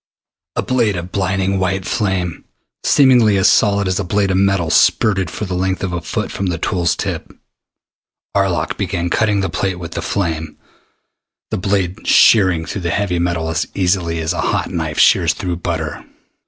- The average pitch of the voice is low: Yes, very low, 95 Hz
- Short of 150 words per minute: No, average, 180 wpm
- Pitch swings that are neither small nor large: No, narrow, 2.3 semitones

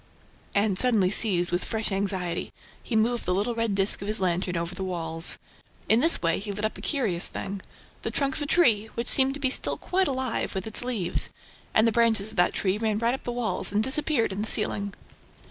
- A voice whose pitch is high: Yes, high, 215 Hz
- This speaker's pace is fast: Yes, fast, 215 wpm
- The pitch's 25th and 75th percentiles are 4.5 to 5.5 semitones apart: No, average, 4.0 semitones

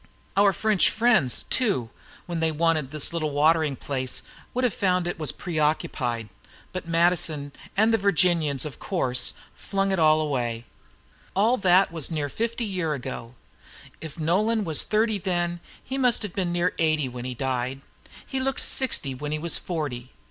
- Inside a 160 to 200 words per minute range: Yes, average, 165 wpm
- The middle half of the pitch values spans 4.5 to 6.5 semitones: Yes, wide, 5.4 semitones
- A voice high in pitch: No, medium, 165 Hz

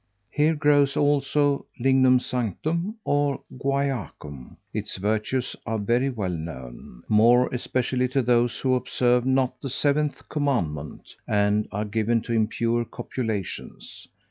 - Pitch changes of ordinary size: Yes, average, 4.3 semitones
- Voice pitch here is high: No, low, 125 Hz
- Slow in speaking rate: Yes, slow, 120 wpm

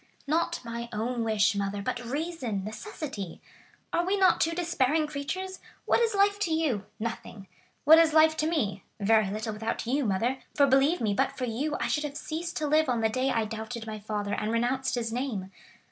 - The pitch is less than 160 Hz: No, very high, 250 Hz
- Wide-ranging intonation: Yes, wide, 6.2 semitones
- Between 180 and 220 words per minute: Yes, average, 190 wpm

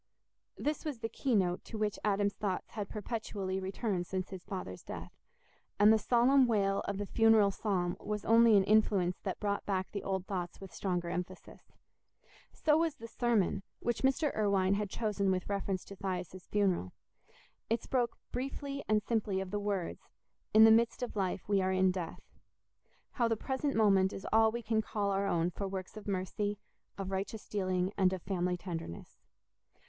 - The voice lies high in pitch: Yes, high, 200 Hz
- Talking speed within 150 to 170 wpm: No, average, 180 wpm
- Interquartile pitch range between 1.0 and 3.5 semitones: Yes, average, 2.8 semitones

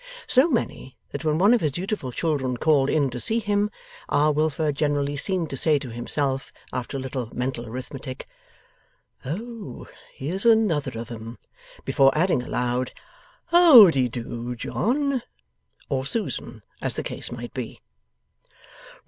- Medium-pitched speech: Yes, medium, 145 Hz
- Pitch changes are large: Yes, wide, 7.0 semitones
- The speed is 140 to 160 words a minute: Yes, average, 145 wpm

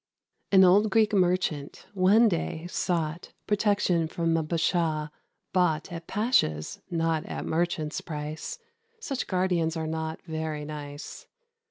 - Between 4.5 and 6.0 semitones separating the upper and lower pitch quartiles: No, average, 3.0 semitones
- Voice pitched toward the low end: No, medium, 165 Hz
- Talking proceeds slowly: Yes, slow, 125 wpm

